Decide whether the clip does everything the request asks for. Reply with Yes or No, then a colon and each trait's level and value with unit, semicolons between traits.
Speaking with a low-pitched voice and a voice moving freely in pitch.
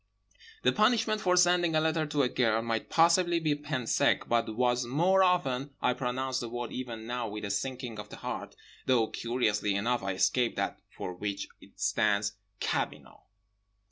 Yes: low, 125 Hz; wide, 6.0 semitones